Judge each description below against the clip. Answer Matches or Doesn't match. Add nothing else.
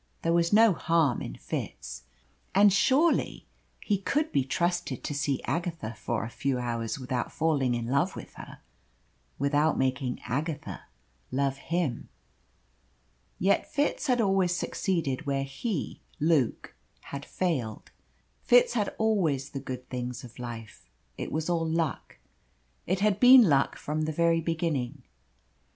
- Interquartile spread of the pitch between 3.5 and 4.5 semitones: Doesn't match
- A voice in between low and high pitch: Matches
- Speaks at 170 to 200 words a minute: Doesn't match